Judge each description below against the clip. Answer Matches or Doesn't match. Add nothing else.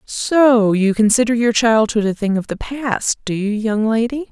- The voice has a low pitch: Doesn't match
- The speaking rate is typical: Matches